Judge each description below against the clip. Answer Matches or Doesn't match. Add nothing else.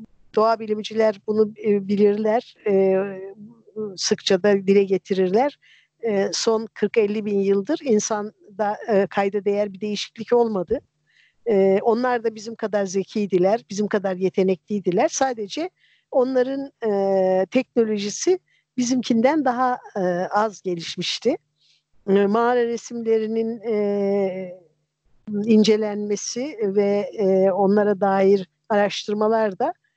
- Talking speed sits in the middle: Doesn't match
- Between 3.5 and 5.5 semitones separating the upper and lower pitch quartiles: Doesn't match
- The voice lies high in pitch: Matches